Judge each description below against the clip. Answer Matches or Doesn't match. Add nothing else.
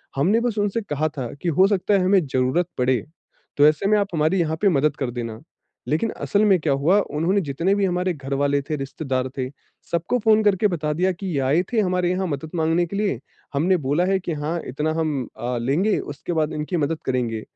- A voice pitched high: Doesn't match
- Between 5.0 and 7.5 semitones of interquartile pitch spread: Matches